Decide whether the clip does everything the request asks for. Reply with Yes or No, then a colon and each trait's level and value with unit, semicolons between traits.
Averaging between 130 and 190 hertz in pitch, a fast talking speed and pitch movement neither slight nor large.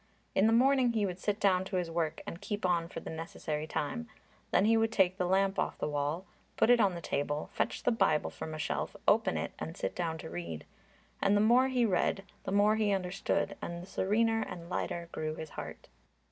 Yes: medium, 185 Hz; fast, 225 wpm; average, 4.8 semitones